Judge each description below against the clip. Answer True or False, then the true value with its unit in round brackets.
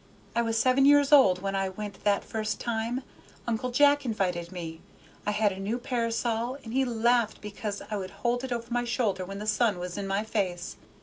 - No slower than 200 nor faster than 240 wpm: True (205 wpm)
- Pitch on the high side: True (220 Hz)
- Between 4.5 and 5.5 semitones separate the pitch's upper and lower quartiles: False (3.5 semitones)